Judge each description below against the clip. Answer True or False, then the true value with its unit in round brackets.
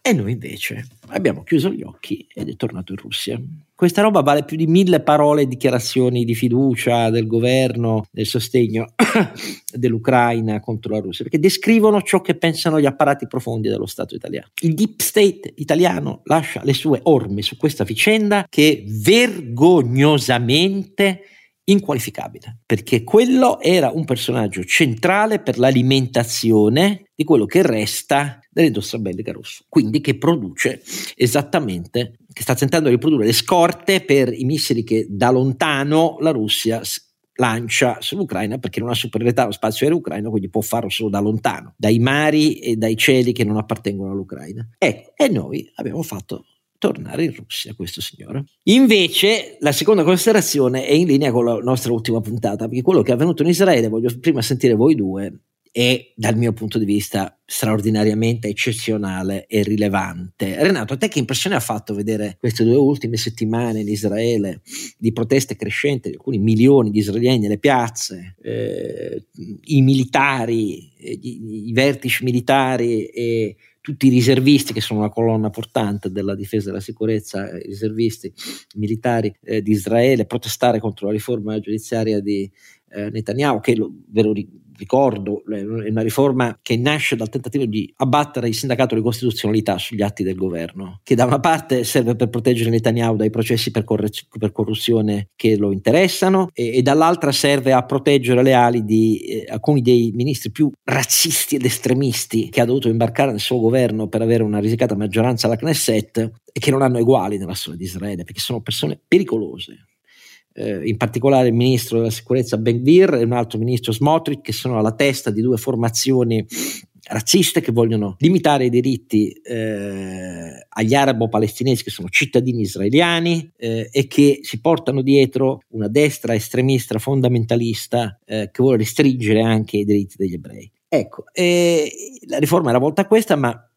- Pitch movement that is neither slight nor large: True (4.2 semitones)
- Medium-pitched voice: False (120 Hz)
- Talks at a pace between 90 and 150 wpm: False (160 wpm)